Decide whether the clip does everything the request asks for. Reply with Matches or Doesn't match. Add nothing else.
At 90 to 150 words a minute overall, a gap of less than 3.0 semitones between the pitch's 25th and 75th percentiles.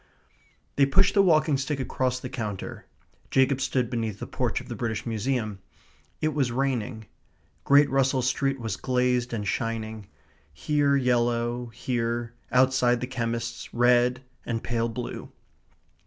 Matches